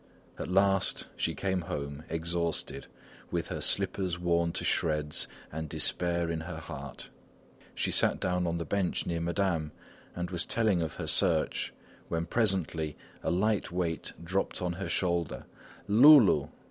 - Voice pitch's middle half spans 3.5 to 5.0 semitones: No, narrow, 2.6 semitones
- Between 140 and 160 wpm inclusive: Yes, average, 145 wpm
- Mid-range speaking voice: No, very low, 85 Hz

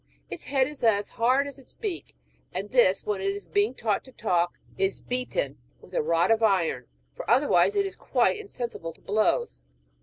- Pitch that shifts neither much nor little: No, wide, 5.8 semitones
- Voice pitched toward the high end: Yes, high, 225 Hz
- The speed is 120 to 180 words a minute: No, average, 190 wpm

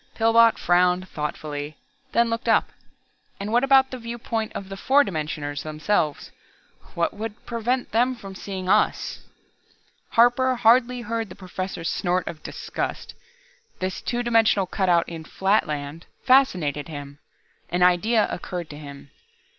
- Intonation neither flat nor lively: No, wide, 5.8 semitones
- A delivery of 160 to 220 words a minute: No, slow, 135 wpm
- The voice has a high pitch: Yes, high, 195 Hz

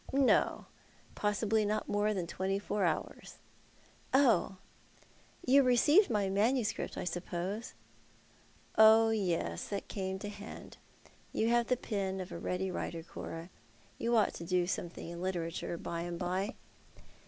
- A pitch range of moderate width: Yes, average, 3.7 semitones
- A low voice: No, high, 195 Hz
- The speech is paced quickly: No, average, 155 wpm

